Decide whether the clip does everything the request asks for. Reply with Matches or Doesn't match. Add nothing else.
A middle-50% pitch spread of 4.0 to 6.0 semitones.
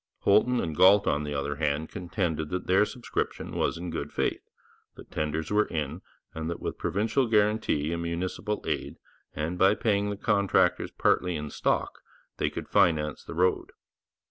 Matches